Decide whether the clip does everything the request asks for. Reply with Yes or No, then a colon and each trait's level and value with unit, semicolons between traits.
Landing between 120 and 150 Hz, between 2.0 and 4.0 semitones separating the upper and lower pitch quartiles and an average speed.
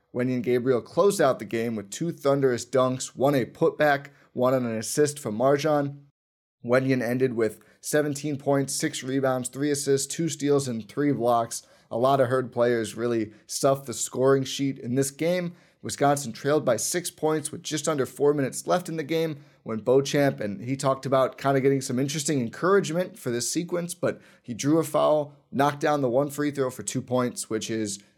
Yes: low, 135 Hz; average, 3.2 semitones; average, 195 wpm